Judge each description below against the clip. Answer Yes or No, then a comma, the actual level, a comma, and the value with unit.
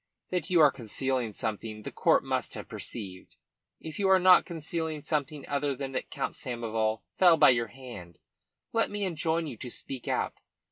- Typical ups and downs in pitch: No, wide, 5.9 semitones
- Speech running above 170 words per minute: Yes, average, 180 wpm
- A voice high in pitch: No, medium, 140 Hz